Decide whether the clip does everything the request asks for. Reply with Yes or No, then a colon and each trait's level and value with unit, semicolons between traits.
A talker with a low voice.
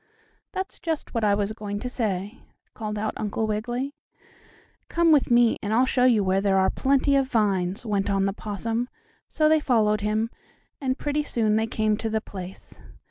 No: high, 220 Hz